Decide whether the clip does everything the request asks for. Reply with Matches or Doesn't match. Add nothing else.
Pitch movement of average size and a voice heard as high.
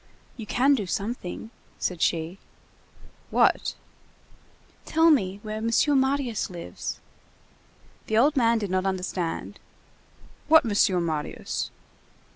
Doesn't match